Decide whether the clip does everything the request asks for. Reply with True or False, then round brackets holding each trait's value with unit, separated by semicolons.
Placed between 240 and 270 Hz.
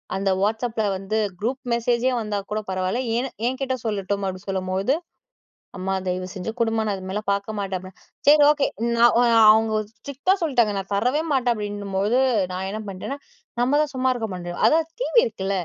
False (215 Hz)